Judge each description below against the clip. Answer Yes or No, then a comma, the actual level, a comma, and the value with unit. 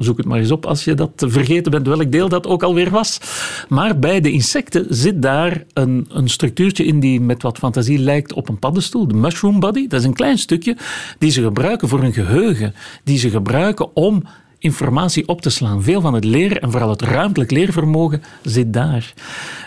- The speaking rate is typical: No, fast, 205 wpm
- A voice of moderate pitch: Yes, medium, 145 Hz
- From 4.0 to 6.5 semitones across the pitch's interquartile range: Yes, wide, 5.6 semitones